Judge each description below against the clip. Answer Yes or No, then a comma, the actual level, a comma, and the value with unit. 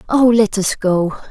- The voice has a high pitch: Yes, high, 210 Hz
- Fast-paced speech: No, average, 185 wpm